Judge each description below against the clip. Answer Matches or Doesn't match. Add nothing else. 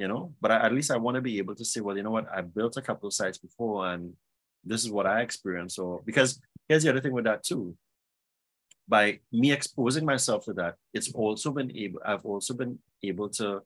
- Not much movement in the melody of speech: Doesn't match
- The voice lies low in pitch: Matches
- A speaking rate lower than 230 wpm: Doesn't match